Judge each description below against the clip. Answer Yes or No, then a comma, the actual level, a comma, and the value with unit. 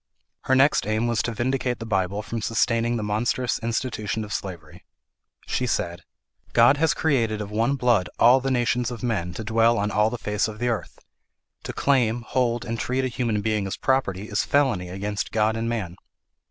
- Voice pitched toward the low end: Yes, low, 115 Hz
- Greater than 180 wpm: Yes, average, 195 wpm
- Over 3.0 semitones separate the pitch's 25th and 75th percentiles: No, average, 2.7 semitones